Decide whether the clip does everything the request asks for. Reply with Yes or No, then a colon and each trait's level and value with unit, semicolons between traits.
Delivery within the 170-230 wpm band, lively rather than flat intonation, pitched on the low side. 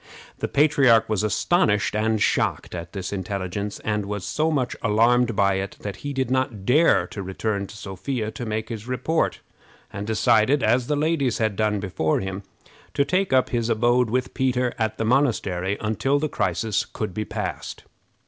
No: average, 175 wpm; average, 4.0 semitones; low, 110 Hz